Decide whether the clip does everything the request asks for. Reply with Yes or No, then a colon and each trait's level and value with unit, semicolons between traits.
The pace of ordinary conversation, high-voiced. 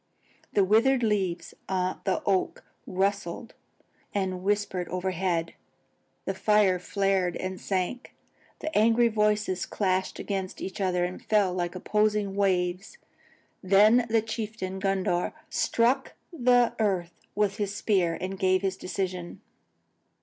No: slow, 125 wpm; high, 195 Hz